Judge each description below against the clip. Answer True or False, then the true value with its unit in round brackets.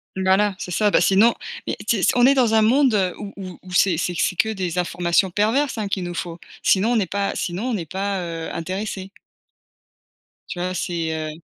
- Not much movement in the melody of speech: False (3.3 semitones)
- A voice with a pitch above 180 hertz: True (190 Hz)